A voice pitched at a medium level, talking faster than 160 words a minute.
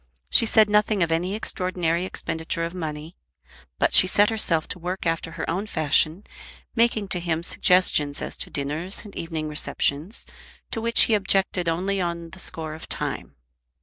Yes: medium, 175 Hz; average, 170 wpm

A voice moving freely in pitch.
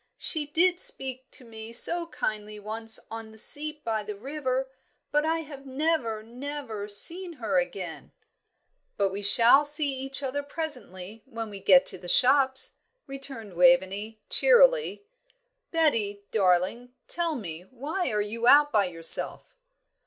Yes: wide, 5.8 semitones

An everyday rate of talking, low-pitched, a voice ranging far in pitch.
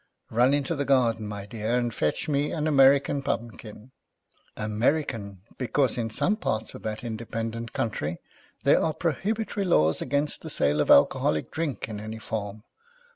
No: average, 155 wpm; low, 115 Hz; average, 4.8 semitones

